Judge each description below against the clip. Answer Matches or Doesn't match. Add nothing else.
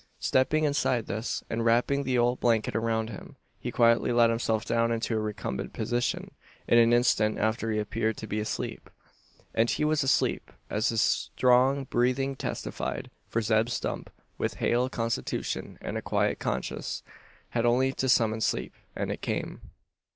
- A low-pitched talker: Matches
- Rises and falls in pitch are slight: Matches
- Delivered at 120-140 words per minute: Doesn't match